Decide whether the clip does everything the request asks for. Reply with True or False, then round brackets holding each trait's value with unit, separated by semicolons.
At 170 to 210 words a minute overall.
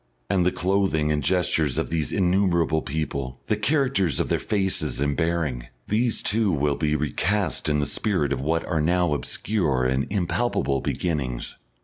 False (160 wpm)